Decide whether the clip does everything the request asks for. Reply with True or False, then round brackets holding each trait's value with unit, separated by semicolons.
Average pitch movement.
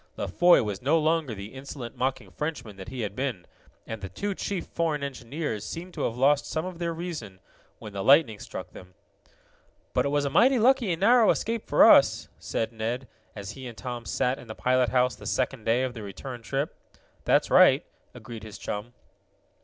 False (6.1 semitones)